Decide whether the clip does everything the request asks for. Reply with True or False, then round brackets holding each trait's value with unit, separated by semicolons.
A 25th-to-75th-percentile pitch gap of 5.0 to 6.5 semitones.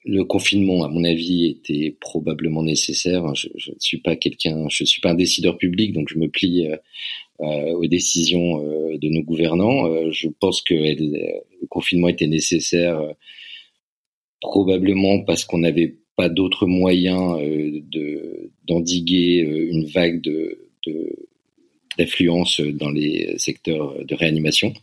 False (2.6 semitones)